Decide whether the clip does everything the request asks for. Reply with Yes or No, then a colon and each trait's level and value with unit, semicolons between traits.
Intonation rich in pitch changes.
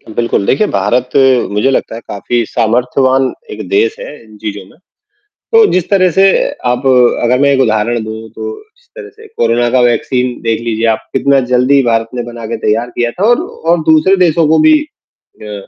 Yes: wide, 6.7 semitones